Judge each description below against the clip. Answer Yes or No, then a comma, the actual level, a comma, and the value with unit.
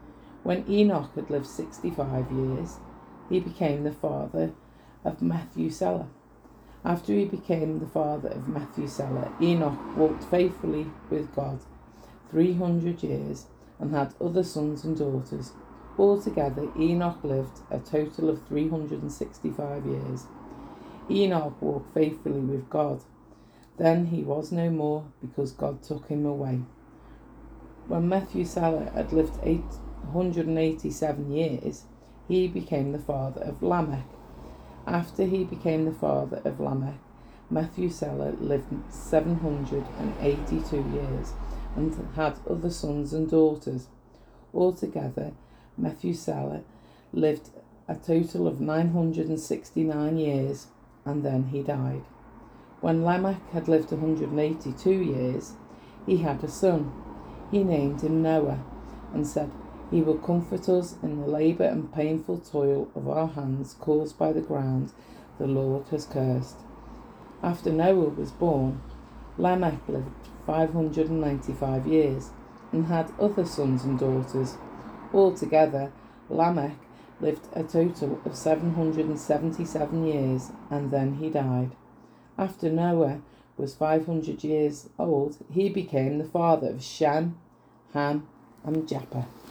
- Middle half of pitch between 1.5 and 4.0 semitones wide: Yes, average, 3.3 semitones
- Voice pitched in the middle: Yes, medium, 150 Hz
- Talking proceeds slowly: Yes, slow, 120 wpm